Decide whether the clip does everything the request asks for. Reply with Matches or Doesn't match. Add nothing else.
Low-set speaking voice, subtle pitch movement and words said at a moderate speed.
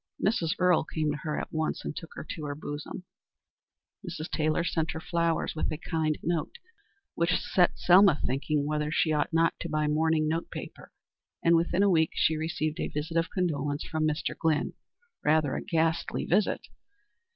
Doesn't match